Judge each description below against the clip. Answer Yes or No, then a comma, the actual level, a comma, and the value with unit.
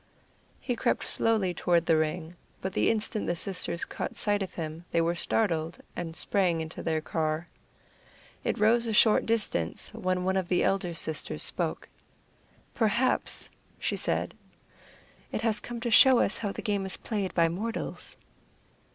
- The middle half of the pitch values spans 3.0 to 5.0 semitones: Yes, average, 4.6 semitones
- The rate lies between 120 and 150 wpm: No, average, 160 wpm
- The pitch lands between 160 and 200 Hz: Yes, medium, 185 Hz